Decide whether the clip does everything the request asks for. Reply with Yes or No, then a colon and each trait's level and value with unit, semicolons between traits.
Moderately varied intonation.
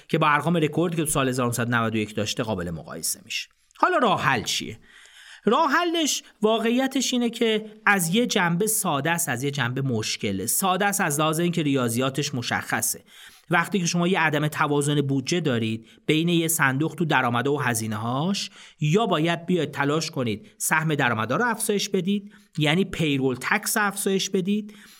No: wide, 7.1 semitones